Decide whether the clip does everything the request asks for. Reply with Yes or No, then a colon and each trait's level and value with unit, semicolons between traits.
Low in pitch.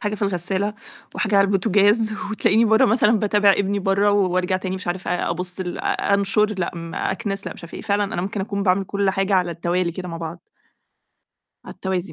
No: high, 195 Hz